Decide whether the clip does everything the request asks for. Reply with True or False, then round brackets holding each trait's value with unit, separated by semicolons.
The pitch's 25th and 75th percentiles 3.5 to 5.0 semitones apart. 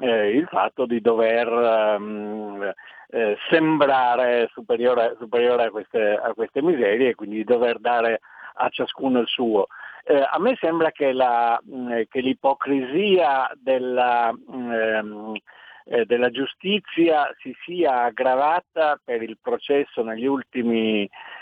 False (3.0 semitones)